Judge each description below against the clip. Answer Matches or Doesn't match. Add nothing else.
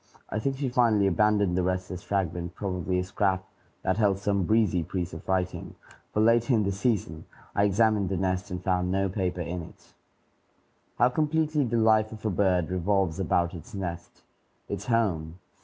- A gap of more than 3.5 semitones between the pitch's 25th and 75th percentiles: Doesn't match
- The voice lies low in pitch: Matches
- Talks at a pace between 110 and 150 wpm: Doesn't match